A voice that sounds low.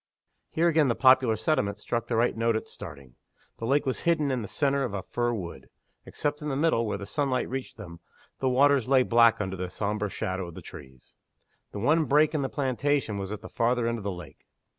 Yes: low, 120 Hz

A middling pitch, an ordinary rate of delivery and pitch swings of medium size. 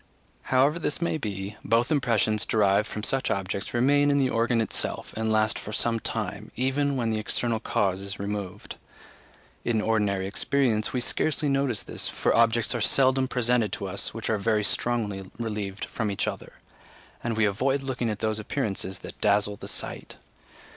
No: low, 110 Hz; average, 175 wpm; average, 3.4 semitones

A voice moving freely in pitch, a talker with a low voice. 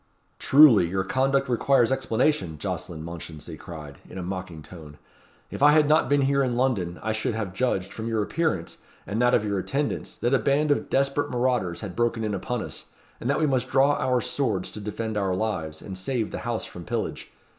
Yes: wide, 6.4 semitones; low, 115 Hz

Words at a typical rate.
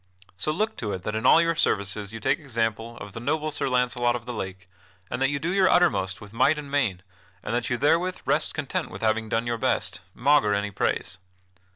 No: fast, 225 wpm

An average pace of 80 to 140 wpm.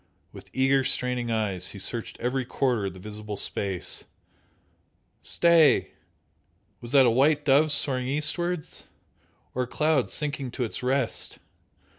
Yes: slow, 135 wpm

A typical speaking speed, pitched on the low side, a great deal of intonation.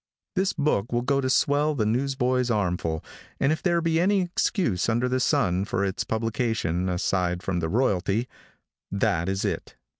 Yes: average, 170 wpm; low, 115 Hz; wide, 6.5 semitones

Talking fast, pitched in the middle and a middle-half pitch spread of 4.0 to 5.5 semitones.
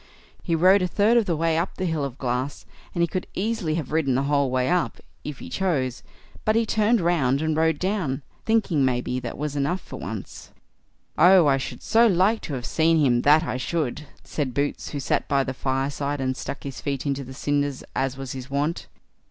Yes: fast, 215 wpm; medium, 145 Hz; average, 4.5 semitones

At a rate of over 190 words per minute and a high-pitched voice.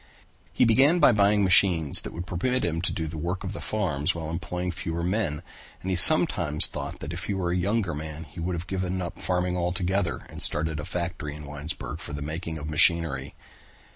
No: fast, 205 wpm; very low, 85 Hz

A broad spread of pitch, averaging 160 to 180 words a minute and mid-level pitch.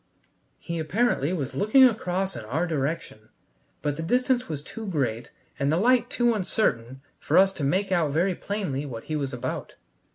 Yes: wide, 6.4 semitones; average, 175 wpm; medium, 165 Hz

